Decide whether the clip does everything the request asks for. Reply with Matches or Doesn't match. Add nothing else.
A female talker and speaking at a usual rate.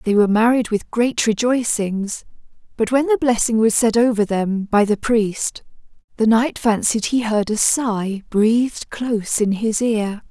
Matches